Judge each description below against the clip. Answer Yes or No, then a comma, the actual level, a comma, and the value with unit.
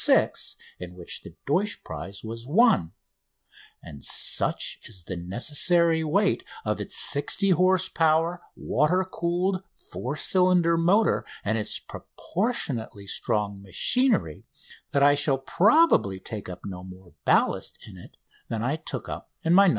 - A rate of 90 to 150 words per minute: Yes, average, 145 wpm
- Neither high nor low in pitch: Yes, medium, 145 Hz